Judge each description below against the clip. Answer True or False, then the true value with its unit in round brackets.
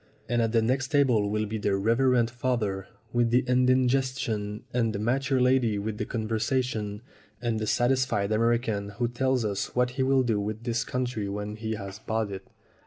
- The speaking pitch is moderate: False (115 Hz)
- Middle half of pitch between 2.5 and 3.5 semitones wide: True (3.2 semitones)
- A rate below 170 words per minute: False (180 wpm)